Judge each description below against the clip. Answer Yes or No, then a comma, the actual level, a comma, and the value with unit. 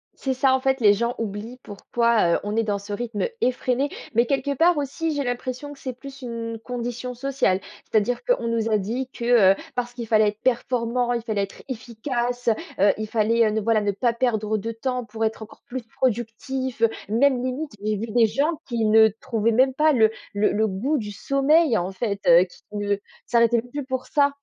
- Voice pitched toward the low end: No, high, 235 Hz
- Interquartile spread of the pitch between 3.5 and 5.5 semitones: No, average, 3.1 semitones